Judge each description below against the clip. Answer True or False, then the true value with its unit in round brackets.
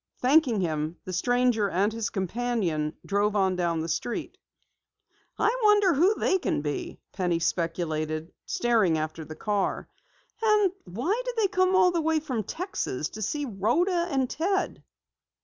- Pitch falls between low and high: False (220 Hz)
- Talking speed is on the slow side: False (150 wpm)